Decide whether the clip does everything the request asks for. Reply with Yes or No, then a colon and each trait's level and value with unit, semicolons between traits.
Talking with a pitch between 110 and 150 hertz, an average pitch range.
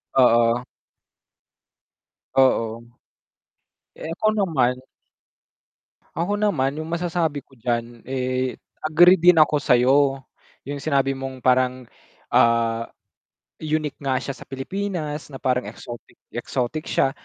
Yes: low, 135 Hz; average, 3.8 semitones